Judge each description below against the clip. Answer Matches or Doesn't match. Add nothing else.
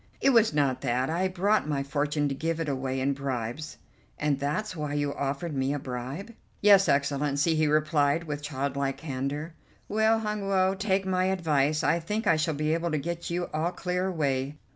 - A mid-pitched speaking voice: Matches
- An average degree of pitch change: Matches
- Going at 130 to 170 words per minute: Doesn't match